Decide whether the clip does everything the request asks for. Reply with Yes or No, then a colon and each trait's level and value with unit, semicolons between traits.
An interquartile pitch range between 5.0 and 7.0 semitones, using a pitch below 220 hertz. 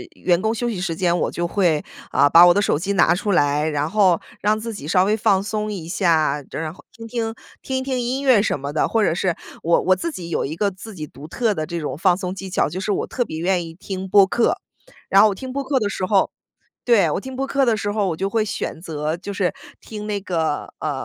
No: average, 4.4 semitones; high, 190 Hz